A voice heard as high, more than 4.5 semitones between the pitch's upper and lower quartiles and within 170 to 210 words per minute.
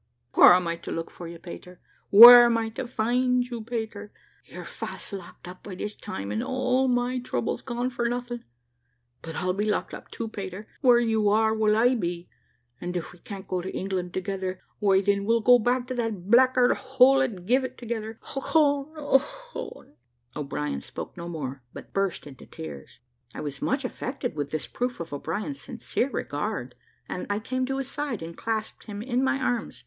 Yes: high, 220 Hz; wide, 5.5 semitones; average, 190 wpm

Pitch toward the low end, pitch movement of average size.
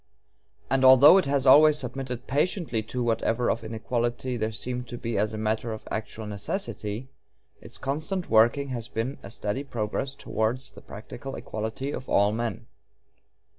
Yes: low, 120 Hz; average, 3.5 semitones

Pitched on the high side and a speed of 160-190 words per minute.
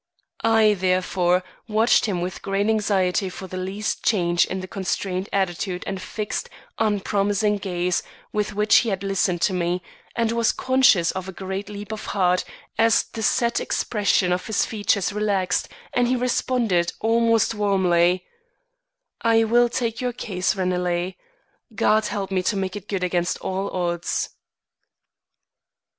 No: high, 195 Hz; average, 150 wpm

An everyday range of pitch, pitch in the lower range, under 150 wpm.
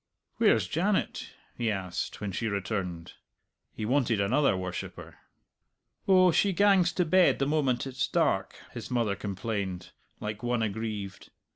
No: wide, 5.8 semitones; low, 110 Hz; slow, 135 wpm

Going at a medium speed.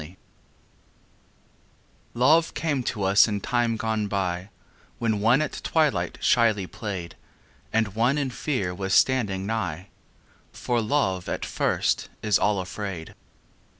No: slow, 125 wpm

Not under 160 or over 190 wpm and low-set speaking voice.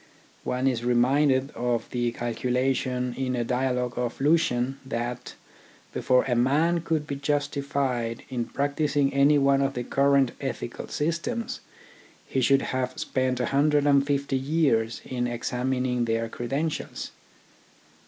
No: slow, 135 wpm; low, 130 Hz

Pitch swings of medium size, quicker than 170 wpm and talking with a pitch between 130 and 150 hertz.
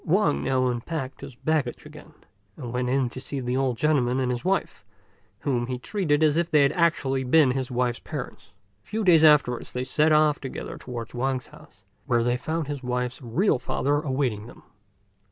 Yes: average, 3.5 semitones; average, 190 wpm; low, 135 Hz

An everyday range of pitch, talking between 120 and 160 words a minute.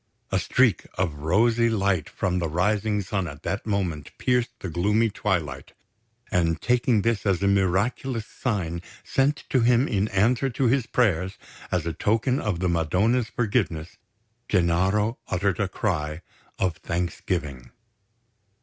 Yes: average, 4.8 semitones; average, 140 wpm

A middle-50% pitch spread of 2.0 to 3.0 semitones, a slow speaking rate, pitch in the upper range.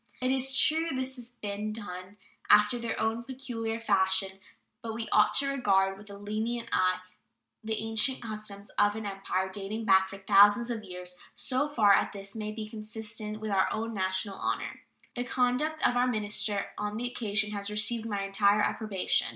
No: average, 2.7 semitones; average, 180 wpm; high, 215 Hz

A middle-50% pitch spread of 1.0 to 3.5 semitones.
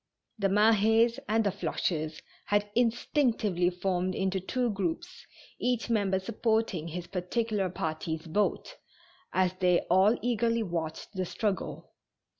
No: average, 3.9 semitones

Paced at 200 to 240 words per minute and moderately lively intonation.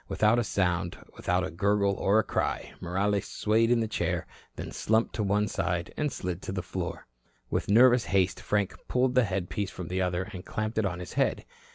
Yes: fast, 205 wpm; average, 3.2 semitones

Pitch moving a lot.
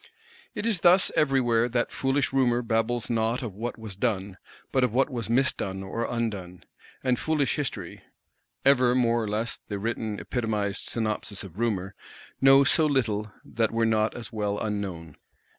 No: average, 3.5 semitones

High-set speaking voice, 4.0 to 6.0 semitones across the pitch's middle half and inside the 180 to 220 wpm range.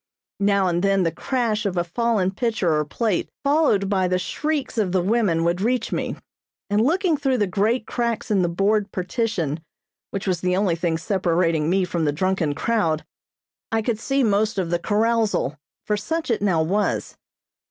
Yes: high, 200 Hz; average, 4.4 semitones; average, 185 wpm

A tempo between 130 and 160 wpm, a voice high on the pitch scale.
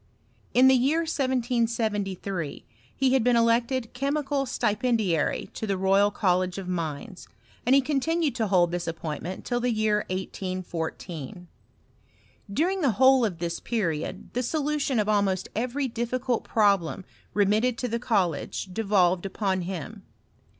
Yes: slow, 135 wpm; high, 215 Hz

